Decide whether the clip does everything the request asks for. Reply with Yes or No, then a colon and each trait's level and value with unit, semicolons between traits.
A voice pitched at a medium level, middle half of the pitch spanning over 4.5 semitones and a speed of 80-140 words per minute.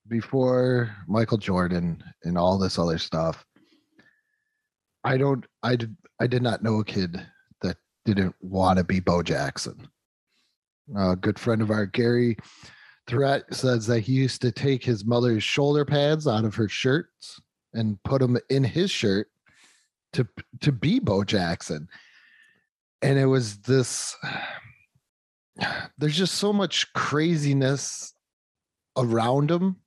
No: low, 125 Hz; average, 5.0 semitones; slow, 135 wpm